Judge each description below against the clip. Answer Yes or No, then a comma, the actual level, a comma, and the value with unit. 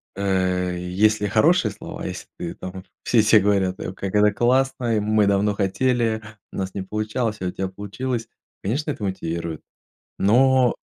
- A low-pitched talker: Yes, low, 105 Hz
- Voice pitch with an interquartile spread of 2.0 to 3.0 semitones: No, average, 3.4 semitones